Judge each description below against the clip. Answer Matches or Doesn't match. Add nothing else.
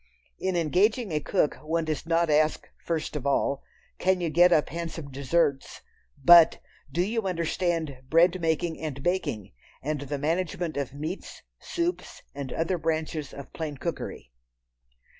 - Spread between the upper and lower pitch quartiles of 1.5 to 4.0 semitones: Matches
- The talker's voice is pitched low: Doesn't match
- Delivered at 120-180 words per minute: Matches